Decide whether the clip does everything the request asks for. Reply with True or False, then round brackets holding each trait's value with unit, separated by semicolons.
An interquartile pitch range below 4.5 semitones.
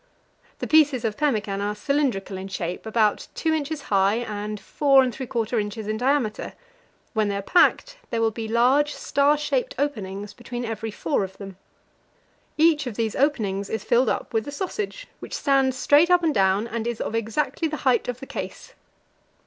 False (5.4 semitones)